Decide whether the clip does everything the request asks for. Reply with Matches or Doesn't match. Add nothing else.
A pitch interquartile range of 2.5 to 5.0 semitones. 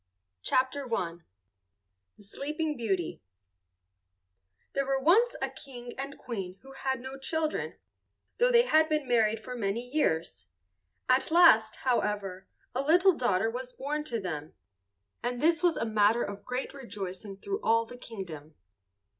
Doesn't match